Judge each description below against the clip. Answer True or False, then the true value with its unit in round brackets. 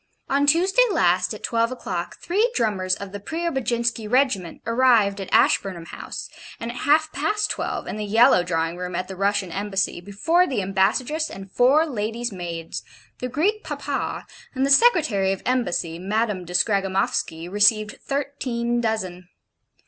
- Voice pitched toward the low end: False (215 Hz)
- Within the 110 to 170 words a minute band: True (155 wpm)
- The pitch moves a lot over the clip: True (5.9 semitones)